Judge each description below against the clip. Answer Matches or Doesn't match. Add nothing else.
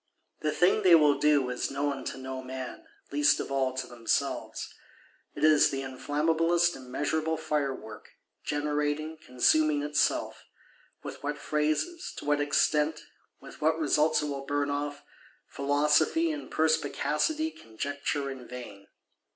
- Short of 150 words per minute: Matches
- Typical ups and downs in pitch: Doesn't match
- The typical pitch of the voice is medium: Matches